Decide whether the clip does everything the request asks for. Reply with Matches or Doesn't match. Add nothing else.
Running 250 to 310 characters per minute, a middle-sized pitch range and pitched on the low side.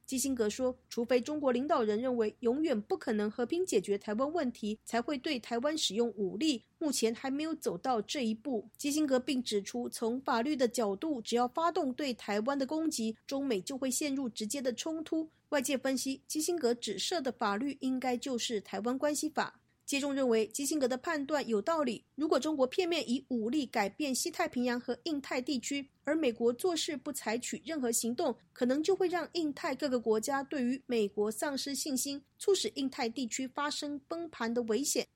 Doesn't match